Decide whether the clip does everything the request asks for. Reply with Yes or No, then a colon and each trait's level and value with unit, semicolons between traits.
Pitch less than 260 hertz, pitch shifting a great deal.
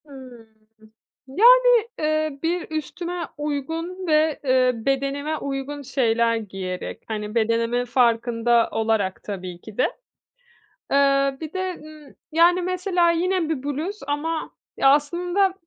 No: very high, 285 Hz; wide, 5.9 semitones